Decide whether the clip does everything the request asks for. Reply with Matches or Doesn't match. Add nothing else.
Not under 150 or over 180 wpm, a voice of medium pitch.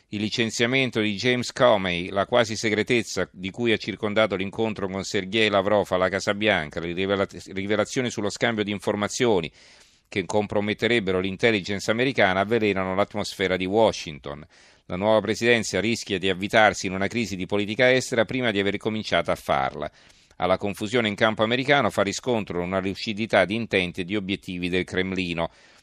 Doesn't match